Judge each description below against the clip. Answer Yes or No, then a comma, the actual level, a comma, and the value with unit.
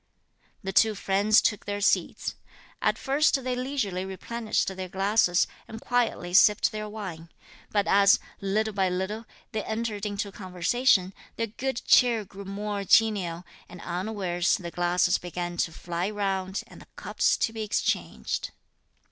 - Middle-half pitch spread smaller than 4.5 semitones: Yes, average, 3.0 semitones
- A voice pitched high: Yes, high, 200 Hz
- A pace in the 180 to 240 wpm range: No, average, 150 wpm